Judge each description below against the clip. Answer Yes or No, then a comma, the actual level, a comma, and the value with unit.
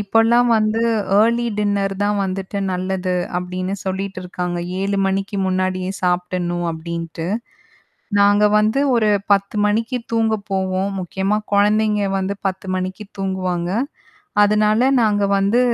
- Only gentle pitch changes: Yes, narrow, 2.3 semitones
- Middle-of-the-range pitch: No, high, 195 Hz